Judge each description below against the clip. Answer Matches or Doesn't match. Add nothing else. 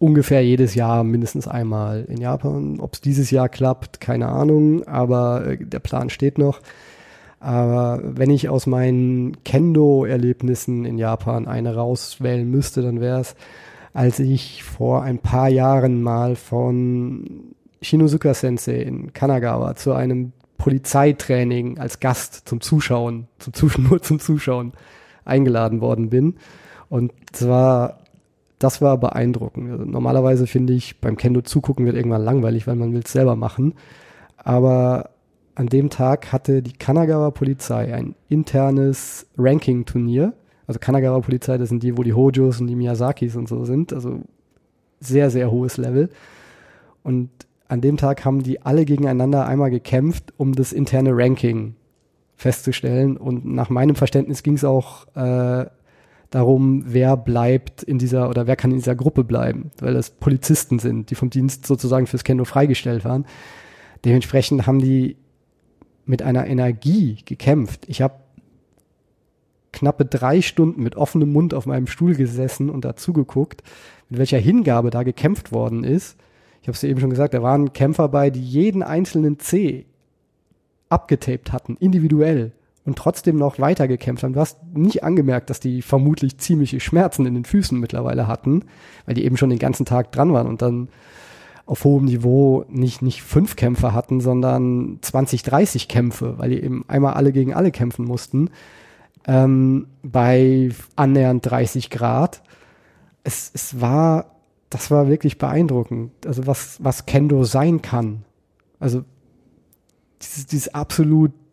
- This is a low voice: Matches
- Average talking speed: Matches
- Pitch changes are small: Matches